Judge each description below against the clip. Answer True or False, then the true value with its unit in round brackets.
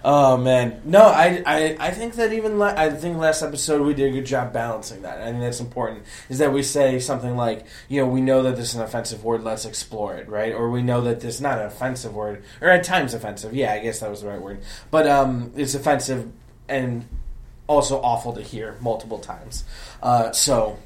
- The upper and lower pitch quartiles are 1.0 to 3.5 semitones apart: False (4.1 semitones)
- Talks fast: True (235 wpm)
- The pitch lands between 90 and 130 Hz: True (120 Hz)